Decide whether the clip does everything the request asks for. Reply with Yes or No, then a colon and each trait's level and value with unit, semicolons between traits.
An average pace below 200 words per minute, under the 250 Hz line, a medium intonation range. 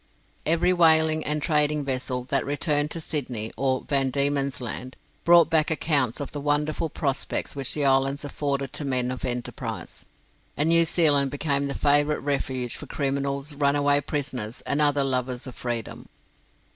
No: average, 160 wpm; medium, 140 Hz; narrow, 2.2 semitones